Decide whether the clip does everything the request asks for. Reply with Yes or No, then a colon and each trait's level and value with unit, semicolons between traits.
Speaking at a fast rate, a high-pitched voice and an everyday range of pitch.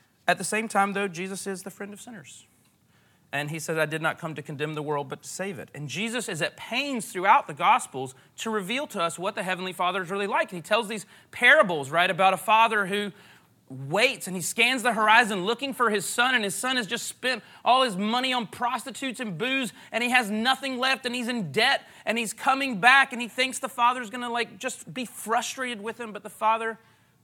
Yes: fast, 235 wpm; high, 220 Hz; average, 4.9 semitones